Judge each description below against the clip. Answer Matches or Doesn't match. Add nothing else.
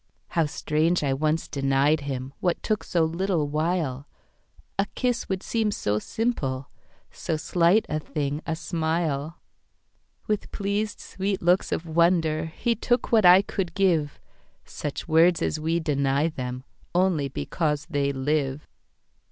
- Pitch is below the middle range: Doesn't match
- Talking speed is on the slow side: Matches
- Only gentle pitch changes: Doesn't match